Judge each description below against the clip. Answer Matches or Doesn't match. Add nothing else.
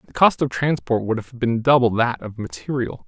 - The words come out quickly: Matches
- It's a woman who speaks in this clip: Doesn't match